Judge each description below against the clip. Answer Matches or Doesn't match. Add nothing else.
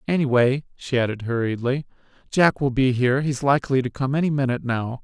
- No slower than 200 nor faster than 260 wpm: Doesn't match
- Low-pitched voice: Matches